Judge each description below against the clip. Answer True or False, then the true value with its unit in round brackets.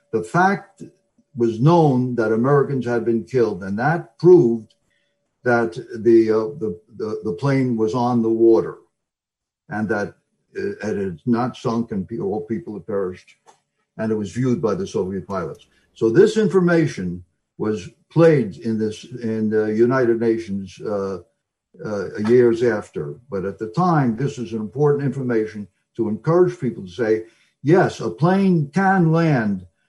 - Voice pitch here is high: False (120 Hz)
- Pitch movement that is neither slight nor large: False (5.9 semitones)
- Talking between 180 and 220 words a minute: False (155 wpm)